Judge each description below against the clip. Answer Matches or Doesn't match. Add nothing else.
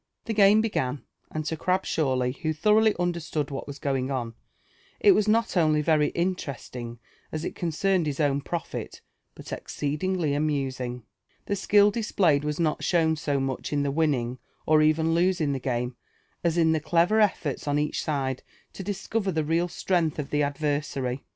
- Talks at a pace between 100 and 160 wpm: Doesn't match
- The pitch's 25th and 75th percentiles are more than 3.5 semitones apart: Matches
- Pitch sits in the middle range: Matches